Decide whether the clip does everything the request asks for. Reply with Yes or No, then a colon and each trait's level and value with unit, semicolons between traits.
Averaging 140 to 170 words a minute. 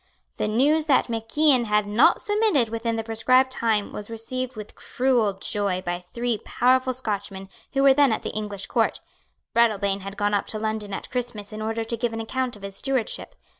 No: average, 200 wpm